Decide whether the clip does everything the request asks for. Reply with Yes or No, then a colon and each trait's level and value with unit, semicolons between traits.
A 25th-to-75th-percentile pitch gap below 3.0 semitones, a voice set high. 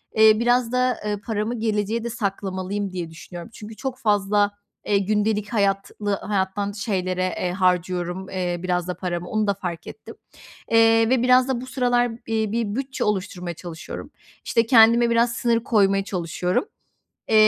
No: average, 3.6 semitones; high, 210 Hz